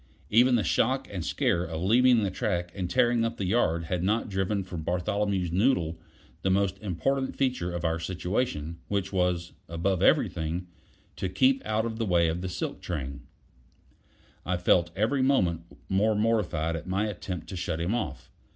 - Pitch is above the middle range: No, very low, 95 Hz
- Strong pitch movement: No, average, 4.1 semitones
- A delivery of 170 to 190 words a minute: Yes, average, 175 wpm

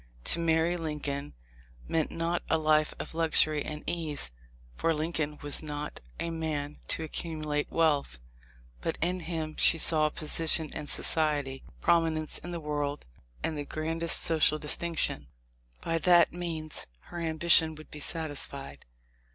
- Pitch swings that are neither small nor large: No, narrow, 1.7 semitones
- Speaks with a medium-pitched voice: Yes, medium, 155 Hz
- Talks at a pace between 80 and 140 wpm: No, average, 150 wpm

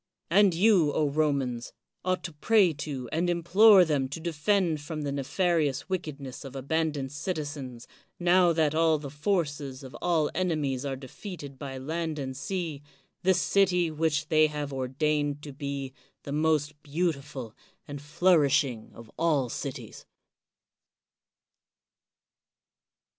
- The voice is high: No, medium, 150 Hz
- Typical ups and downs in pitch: Yes, average, 3.5 semitones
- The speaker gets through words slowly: Yes, slow, 125 wpm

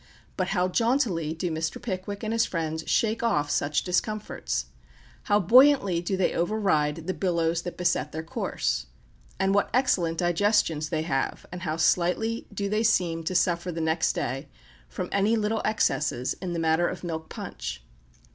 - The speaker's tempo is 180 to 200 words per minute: No, average, 165 wpm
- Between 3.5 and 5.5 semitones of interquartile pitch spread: Yes, average, 4.2 semitones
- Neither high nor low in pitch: Yes, medium, 180 Hz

